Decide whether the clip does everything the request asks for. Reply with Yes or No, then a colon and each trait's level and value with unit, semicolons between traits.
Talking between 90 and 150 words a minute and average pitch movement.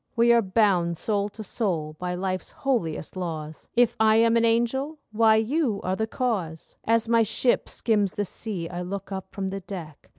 No: average, 185 wpm; average, 4.1 semitones